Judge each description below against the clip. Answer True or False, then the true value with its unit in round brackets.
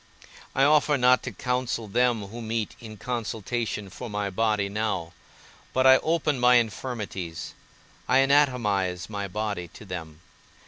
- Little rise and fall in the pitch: False (3.9 semitones)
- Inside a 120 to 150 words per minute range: True (140 wpm)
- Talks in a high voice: False (110 Hz)